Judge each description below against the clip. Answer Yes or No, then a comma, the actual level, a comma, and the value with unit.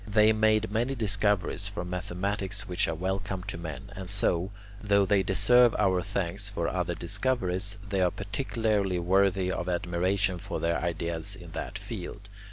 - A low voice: Yes, very low, 95 Hz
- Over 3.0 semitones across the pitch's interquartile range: No, narrow, 2.4 semitones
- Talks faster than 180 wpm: No, average, 160 wpm